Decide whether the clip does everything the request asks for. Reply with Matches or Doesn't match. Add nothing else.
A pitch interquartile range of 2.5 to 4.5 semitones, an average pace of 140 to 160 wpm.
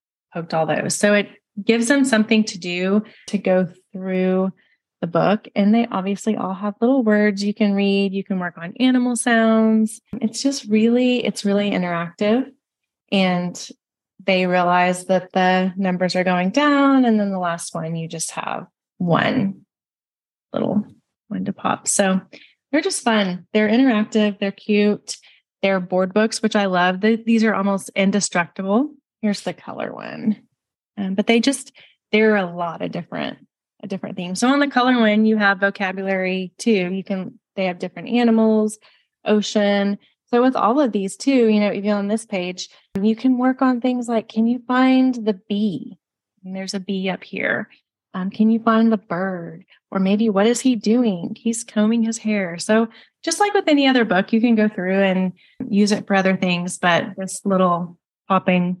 Doesn't match